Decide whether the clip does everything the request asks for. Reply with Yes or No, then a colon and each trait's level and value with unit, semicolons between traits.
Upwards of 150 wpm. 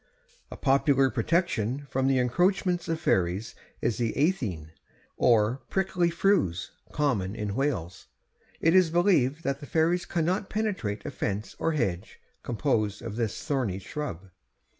No: average, 140 wpm